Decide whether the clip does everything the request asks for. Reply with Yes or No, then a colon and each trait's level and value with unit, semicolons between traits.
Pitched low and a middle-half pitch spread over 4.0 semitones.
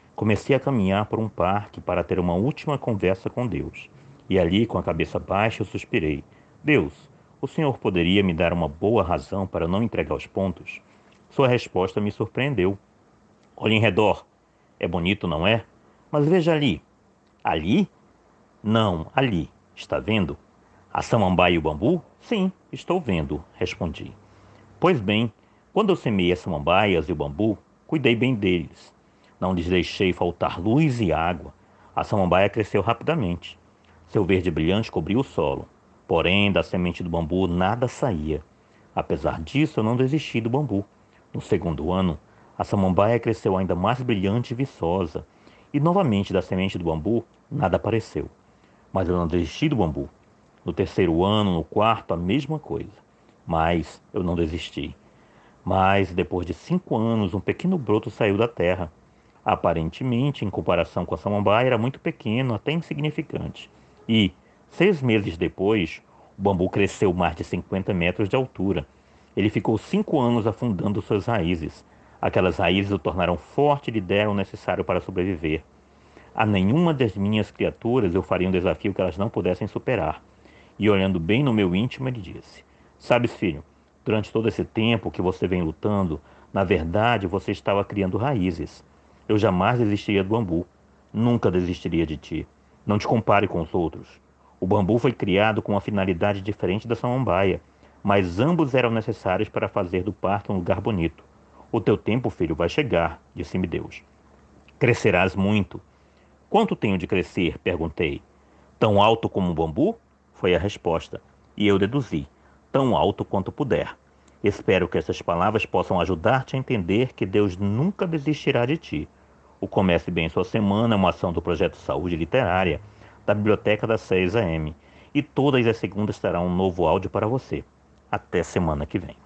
Yes: low, 100 Hz; average, 4.5 semitones